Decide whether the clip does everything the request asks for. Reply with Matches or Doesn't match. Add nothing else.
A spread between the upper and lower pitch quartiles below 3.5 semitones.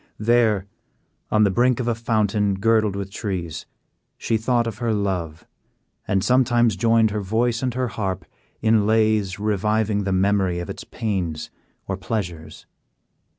Matches